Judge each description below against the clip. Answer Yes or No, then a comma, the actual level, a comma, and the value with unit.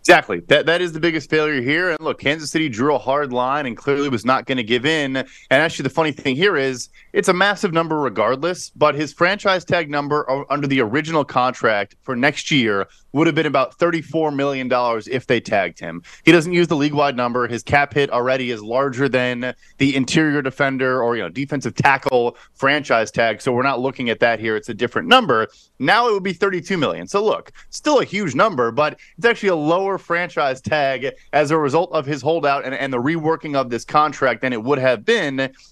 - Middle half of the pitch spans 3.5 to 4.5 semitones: Yes, average, 3.9 semitones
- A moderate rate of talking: No, fast, 220 wpm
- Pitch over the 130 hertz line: Yes, medium, 140 Hz